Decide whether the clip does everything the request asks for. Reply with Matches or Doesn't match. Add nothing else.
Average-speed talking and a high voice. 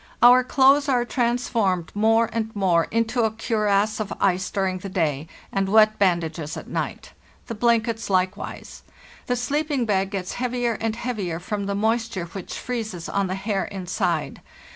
Matches